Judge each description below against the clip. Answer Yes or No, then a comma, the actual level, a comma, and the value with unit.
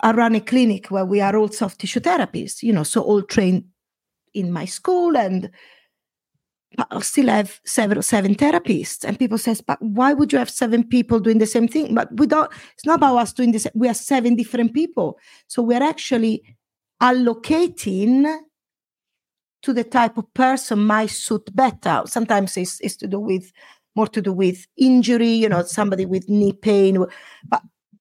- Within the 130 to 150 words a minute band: No, average, 185 wpm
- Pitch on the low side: No, high, 225 Hz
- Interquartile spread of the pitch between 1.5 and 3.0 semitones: No, average, 3.9 semitones